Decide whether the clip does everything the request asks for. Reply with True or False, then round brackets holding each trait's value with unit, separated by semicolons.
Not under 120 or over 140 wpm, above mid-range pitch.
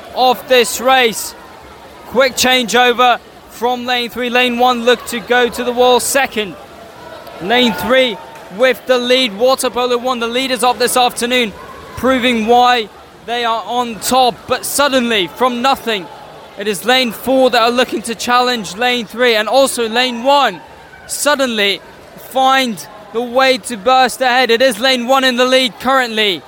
False (160 wpm; 245 Hz)